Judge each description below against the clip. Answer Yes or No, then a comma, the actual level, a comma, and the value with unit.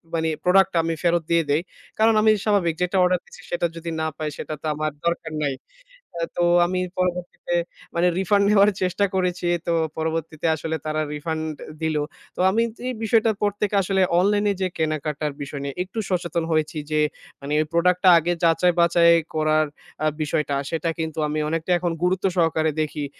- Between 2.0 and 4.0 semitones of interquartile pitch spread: Yes, narrow, 2.6 semitones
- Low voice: No, medium, 170 Hz